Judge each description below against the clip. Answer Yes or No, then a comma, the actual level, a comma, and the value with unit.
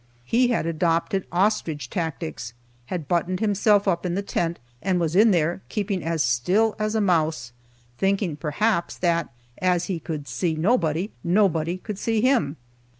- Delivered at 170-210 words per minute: No, average, 155 wpm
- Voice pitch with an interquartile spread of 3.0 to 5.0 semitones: Yes, average, 4.0 semitones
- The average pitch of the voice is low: No, medium, 175 Hz